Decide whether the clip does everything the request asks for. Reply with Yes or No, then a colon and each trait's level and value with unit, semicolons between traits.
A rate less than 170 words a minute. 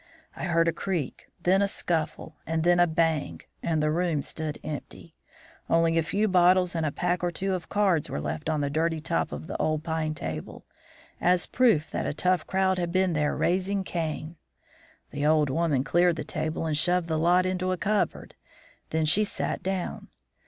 No: average, 195 wpm